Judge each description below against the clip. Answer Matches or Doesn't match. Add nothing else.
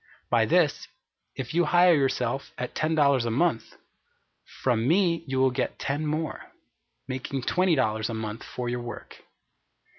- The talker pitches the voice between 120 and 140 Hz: Matches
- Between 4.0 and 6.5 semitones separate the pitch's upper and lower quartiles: Matches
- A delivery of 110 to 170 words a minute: Matches